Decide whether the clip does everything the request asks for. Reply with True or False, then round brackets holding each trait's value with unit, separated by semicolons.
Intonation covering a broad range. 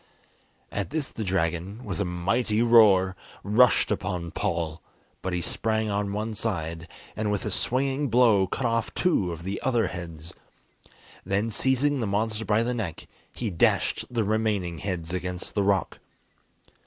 False (4.3 semitones)